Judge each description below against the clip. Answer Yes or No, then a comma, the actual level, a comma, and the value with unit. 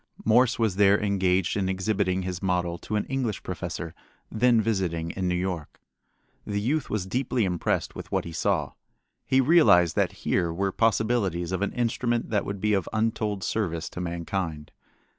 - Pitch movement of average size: Yes, average, 3.8 semitones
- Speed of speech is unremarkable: Yes, average, 170 wpm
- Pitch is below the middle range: Yes, very low, 95 Hz